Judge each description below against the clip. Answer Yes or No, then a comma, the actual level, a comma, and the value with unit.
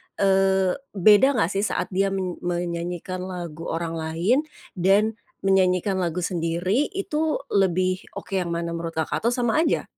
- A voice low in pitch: No, medium, 185 Hz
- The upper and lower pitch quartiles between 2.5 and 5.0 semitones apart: Yes, average, 2.8 semitones